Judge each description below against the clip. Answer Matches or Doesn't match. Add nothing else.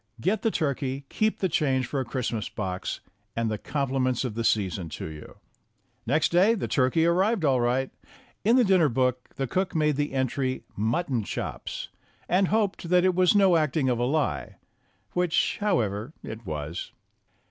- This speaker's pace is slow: Doesn't match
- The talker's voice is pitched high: Doesn't match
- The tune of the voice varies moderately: Doesn't match